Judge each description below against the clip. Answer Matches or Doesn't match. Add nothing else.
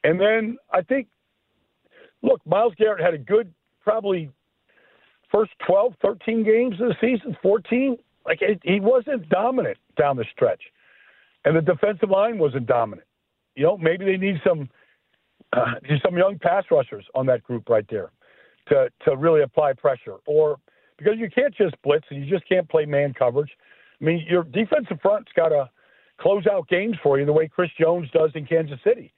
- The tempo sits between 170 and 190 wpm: Matches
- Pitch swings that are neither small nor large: Doesn't match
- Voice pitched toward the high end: Matches